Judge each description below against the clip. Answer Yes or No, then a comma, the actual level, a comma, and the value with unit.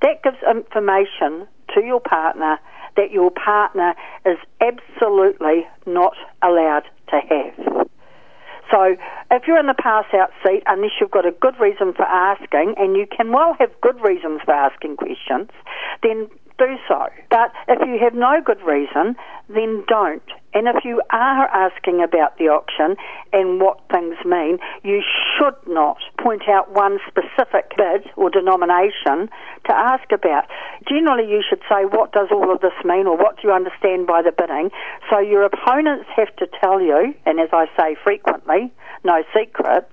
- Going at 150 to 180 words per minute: Yes, average, 165 wpm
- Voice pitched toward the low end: No, high, 205 Hz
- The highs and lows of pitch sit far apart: Yes, wide, 6.1 semitones